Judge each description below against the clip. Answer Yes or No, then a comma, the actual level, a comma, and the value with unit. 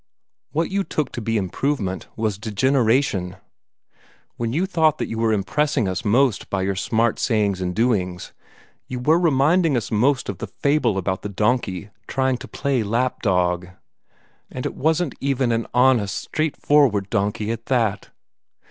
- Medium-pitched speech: No, low, 115 Hz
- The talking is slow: No, average, 155 wpm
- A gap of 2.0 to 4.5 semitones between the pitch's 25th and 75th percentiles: No, wide, 5.4 semitones